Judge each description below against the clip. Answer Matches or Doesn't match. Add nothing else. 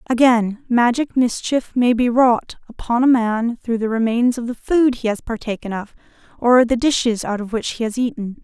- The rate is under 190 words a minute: Doesn't match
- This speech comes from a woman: Matches